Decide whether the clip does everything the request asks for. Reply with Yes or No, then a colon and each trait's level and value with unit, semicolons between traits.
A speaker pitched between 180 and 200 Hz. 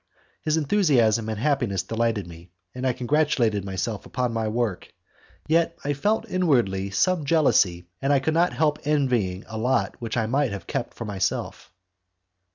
No: low, 120 Hz